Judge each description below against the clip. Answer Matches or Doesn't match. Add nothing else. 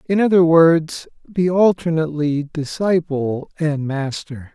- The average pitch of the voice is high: Doesn't match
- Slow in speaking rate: Matches